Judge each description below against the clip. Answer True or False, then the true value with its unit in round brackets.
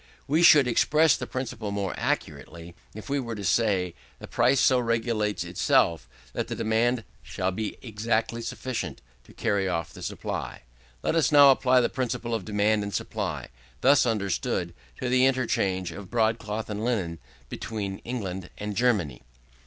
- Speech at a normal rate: True (160 wpm)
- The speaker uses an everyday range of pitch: True (3.9 semitones)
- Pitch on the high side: False (110 Hz)